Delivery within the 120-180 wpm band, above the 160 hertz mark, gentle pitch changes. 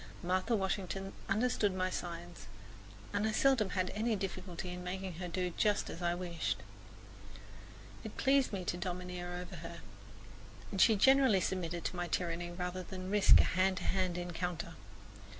Yes: average, 160 wpm; medium, 185 Hz; narrow, 1.9 semitones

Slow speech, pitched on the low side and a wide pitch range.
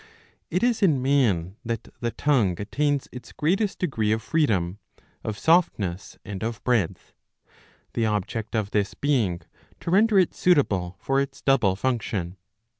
No: average, 145 wpm; low, 115 Hz; wide, 6.3 semitones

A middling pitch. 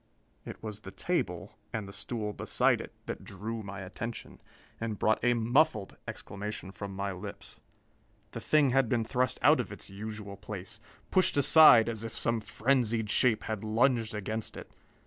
No: low, 110 Hz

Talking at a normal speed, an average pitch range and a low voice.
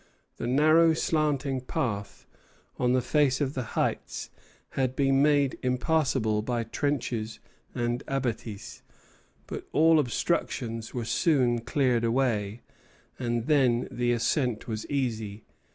No: slow, 120 wpm; average, 3.4 semitones; low, 125 Hz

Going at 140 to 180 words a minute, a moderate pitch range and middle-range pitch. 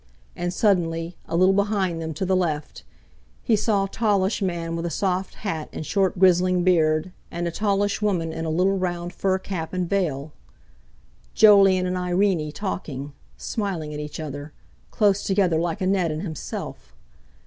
Yes: average, 165 wpm; average, 3.1 semitones; medium, 180 Hz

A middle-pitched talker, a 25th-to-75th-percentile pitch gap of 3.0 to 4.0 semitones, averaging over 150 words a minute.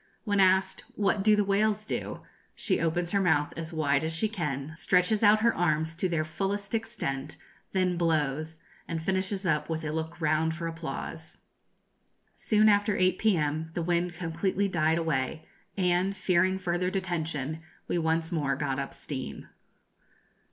Yes: medium, 170 Hz; average, 3.4 semitones; average, 160 wpm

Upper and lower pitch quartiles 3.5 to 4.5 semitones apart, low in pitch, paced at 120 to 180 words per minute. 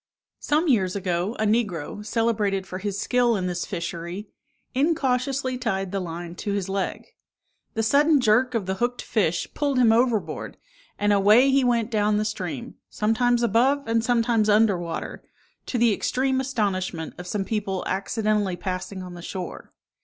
No: average, 4.2 semitones; high, 215 Hz; average, 160 wpm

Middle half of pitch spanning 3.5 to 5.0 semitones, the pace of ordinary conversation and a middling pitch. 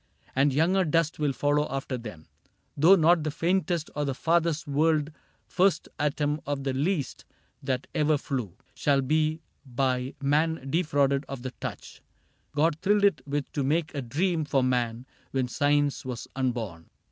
No: average, 3.1 semitones; average, 160 wpm; medium, 145 Hz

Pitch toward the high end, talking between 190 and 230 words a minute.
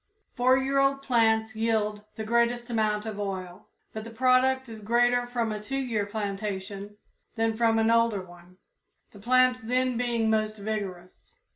No: high, 225 Hz; average, 160 wpm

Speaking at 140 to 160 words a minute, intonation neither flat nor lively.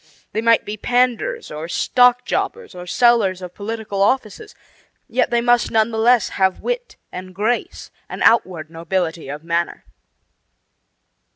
Yes: average, 145 wpm; average, 5.0 semitones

